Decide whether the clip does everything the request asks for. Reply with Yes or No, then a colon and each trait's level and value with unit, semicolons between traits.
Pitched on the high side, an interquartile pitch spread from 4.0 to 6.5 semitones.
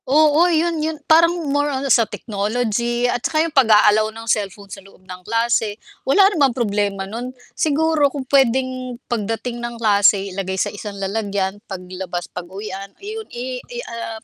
Yes: high, 230 Hz; average, 5.2 semitones